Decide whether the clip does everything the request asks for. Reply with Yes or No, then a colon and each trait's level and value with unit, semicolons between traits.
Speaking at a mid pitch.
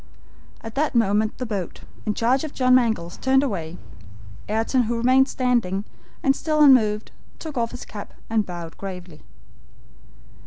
No: high, 230 Hz